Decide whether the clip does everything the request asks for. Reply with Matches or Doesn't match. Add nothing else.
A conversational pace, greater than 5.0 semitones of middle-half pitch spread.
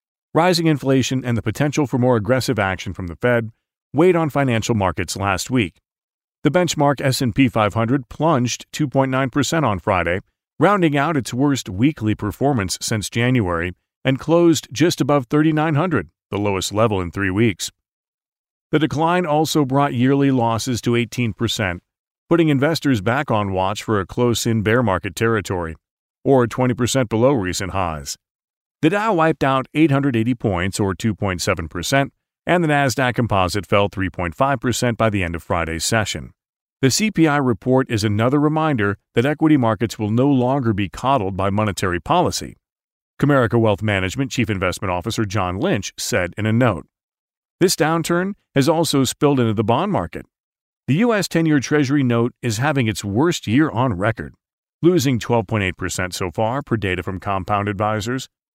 Matches